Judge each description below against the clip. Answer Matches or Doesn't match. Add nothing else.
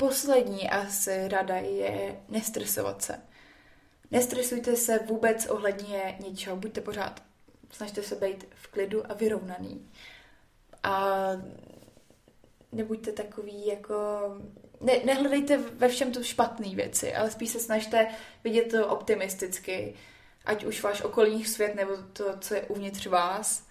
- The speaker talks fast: Doesn't match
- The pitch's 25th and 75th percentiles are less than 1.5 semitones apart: Doesn't match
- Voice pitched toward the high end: Matches